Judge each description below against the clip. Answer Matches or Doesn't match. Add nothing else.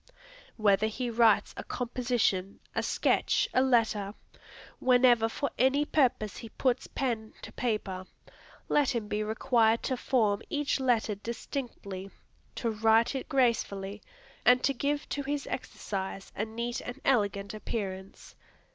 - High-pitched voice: Matches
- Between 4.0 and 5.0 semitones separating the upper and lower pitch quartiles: Doesn't match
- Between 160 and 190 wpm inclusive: Doesn't match